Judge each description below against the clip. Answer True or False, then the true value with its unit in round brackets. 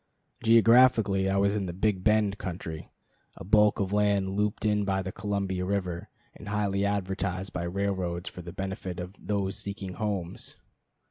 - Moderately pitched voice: False (100 Hz)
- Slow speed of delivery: False (160 wpm)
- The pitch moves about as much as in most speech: False (1.8 semitones)